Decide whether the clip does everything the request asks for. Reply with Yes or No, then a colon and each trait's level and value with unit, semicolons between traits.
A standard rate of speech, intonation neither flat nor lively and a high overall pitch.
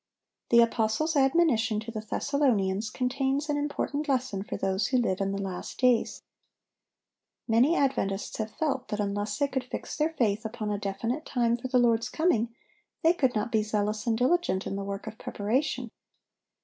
Yes: average, 175 wpm; average, 4.4 semitones; high, 235 Hz